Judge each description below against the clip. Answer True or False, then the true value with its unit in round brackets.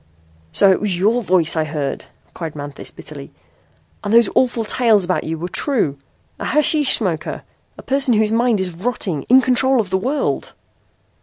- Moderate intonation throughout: False (6.6 semitones)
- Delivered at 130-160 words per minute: False (170 wpm)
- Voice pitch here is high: True (205 Hz)